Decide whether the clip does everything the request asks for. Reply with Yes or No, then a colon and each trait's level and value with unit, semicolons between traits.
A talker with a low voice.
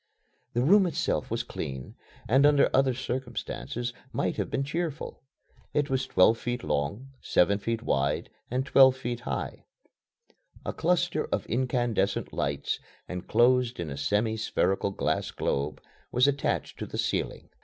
Yes: low, 120 Hz